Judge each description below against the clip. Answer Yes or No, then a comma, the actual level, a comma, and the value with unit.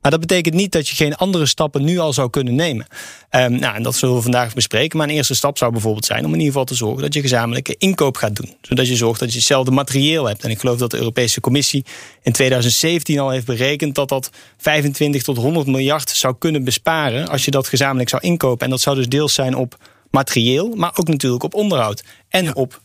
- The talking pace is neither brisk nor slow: No, fast, 240 wpm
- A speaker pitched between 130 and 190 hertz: Yes, low, 135 Hz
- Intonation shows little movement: No, average, 3.3 semitones